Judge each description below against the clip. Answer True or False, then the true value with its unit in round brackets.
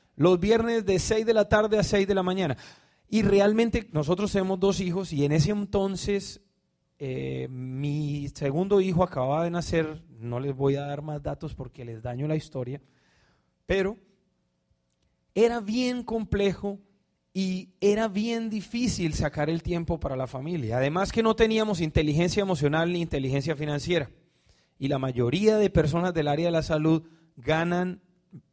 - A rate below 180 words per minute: True (160 wpm)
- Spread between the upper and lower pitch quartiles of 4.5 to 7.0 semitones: True (5.2 semitones)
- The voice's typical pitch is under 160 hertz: False (175 Hz)